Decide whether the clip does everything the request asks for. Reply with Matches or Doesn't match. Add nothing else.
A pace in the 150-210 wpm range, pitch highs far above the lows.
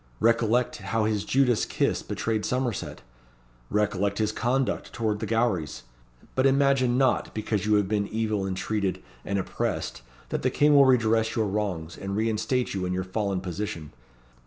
Doesn't match